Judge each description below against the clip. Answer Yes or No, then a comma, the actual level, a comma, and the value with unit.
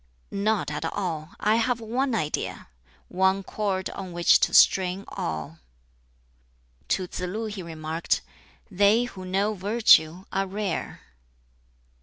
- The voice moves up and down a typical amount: Yes, average, 3.1 semitones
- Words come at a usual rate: No, slow, 125 wpm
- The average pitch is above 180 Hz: Yes, high, 190 Hz